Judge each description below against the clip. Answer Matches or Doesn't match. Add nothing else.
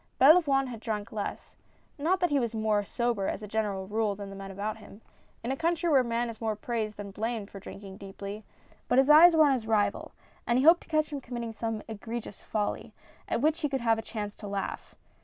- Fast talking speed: Matches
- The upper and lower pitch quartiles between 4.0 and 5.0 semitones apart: Matches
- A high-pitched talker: Matches